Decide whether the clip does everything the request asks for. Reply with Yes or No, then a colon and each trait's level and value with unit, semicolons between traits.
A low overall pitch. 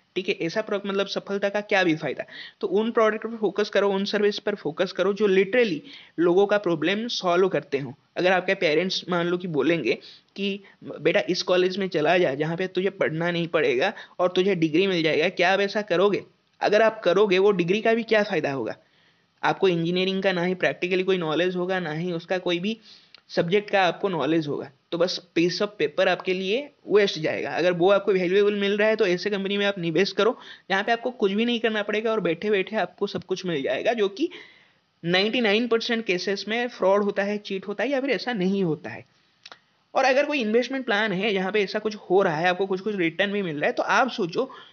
No: high, 195 Hz